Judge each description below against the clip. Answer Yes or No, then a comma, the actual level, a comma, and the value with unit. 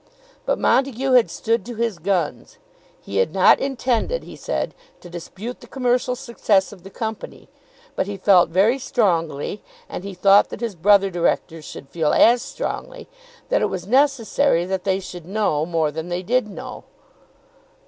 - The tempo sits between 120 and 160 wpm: No, average, 170 wpm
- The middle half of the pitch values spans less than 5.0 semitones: No, wide, 5.4 semitones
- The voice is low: No, high, 200 Hz